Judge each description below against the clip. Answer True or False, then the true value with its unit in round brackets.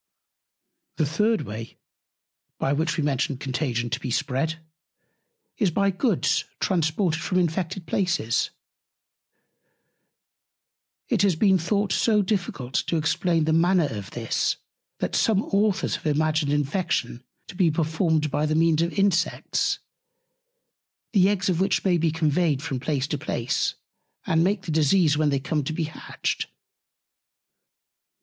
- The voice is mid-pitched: True (160 Hz)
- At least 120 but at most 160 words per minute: True (140 wpm)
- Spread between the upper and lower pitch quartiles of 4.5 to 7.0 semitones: False (4.0 semitones)